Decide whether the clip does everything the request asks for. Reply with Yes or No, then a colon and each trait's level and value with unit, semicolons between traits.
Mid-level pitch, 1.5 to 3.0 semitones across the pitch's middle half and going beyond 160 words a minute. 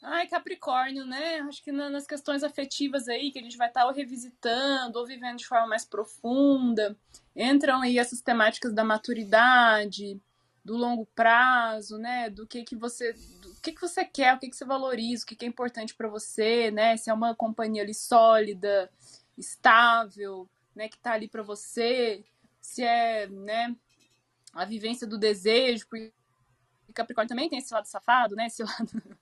No: high, 235 Hz; narrow, 2.6 semitones; average, 170 wpm